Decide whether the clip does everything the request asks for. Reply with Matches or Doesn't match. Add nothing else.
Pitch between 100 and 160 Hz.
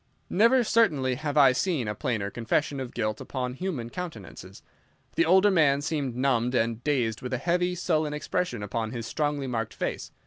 Matches